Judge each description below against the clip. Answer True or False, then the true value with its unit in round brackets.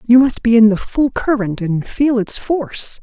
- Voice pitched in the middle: False (235 Hz)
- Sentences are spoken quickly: True (220 wpm)